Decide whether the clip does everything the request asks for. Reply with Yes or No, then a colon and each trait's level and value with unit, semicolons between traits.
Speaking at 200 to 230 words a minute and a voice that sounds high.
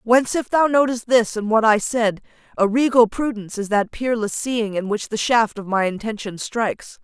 Yes: fast, 205 wpm; high, 225 Hz